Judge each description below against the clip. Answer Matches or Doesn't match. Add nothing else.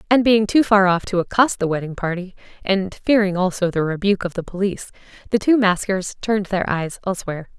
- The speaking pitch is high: Matches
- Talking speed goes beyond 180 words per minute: Matches